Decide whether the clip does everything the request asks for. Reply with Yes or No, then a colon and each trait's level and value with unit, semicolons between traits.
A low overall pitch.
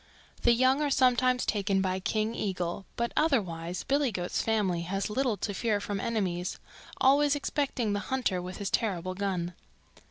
No: high, 210 Hz